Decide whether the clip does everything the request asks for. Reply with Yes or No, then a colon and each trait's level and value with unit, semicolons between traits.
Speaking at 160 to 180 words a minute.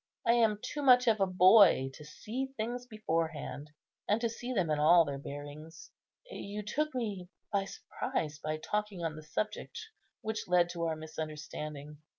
Yes: average, 165 wpm